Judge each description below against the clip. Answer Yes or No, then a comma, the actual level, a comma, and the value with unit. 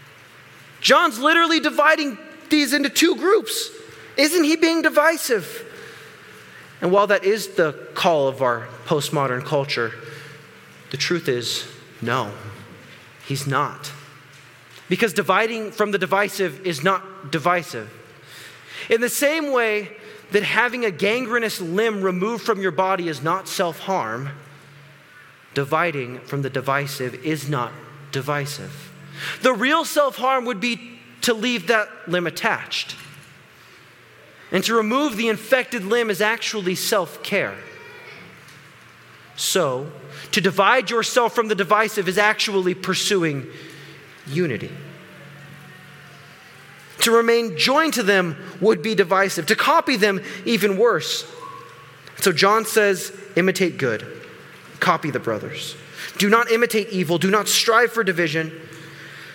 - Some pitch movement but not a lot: No, wide, 7.2 semitones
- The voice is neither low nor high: No, high, 195 Hz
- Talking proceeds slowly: Yes, slow, 120 wpm